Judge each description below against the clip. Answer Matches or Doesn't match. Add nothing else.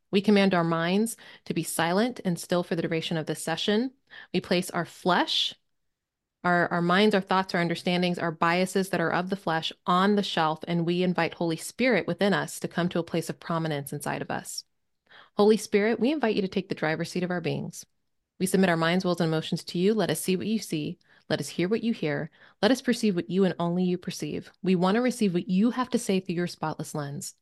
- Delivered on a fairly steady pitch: Doesn't match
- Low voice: Doesn't match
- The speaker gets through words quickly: Matches